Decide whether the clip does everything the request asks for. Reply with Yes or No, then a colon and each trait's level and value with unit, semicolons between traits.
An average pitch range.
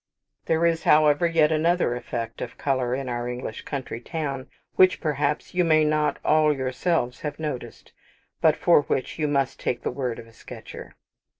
Yes: average, 3.9 semitones